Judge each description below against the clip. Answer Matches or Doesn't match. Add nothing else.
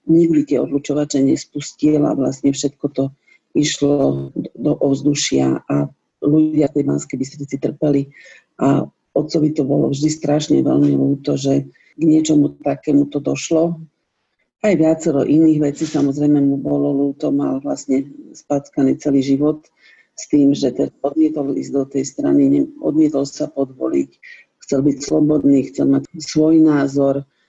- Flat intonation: Matches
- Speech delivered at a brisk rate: Doesn't match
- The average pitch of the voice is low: Doesn't match